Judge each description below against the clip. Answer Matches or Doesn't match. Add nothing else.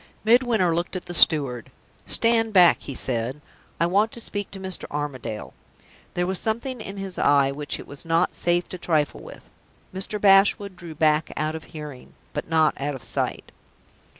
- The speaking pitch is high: Doesn't match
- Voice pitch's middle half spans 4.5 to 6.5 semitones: Matches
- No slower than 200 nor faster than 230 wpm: Doesn't match